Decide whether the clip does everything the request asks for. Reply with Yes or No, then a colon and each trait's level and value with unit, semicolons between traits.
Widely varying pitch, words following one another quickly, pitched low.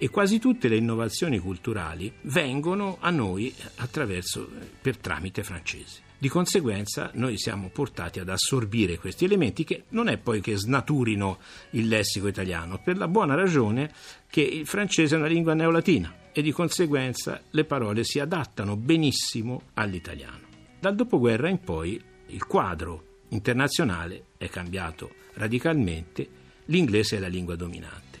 No: wide, 8.8 semitones; average, 140 wpm; low, 115 Hz